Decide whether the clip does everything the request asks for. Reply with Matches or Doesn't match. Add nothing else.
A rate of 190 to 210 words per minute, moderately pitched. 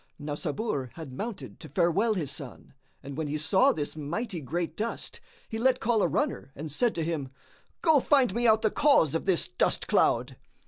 Matches